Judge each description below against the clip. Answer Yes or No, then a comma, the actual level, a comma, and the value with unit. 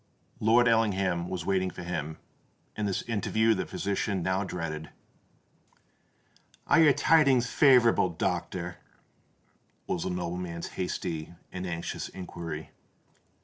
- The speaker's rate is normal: No, slow, 110 wpm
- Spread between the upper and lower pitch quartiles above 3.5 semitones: Yes, average, 4.4 semitones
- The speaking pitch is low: Yes, very low, 95 Hz